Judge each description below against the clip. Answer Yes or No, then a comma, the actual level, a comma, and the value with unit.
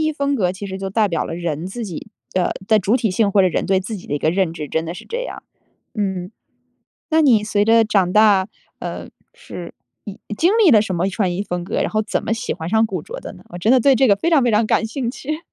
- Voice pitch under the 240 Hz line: Yes, high, 205 Hz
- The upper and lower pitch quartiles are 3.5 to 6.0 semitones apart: Yes, average, 3.8 semitones